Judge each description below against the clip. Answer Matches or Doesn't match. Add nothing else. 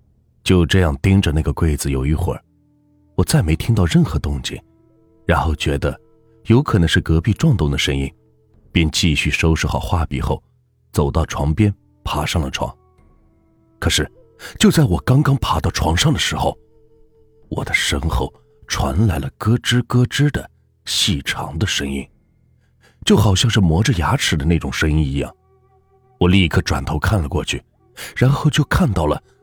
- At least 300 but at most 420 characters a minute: Doesn't match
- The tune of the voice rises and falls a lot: Matches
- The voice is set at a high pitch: Doesn't match